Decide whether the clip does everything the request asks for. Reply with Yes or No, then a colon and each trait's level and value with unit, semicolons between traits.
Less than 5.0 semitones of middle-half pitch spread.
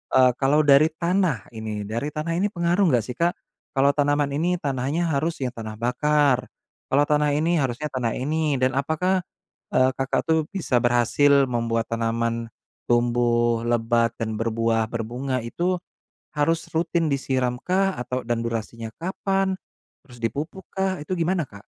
No: average, 5.3 semitones